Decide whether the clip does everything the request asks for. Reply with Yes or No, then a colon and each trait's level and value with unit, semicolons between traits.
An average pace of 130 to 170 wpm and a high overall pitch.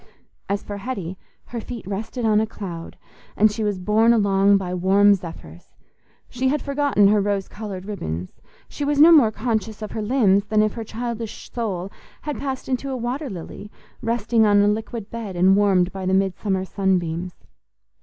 No: average, 185 wpm; high, 210 Hz